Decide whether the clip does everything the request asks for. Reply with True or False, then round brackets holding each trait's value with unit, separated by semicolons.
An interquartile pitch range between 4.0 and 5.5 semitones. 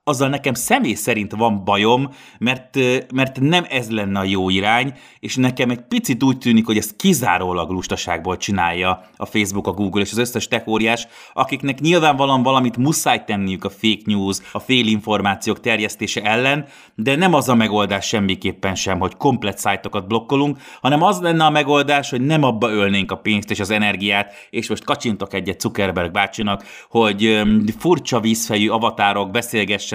True (4.6 semitones)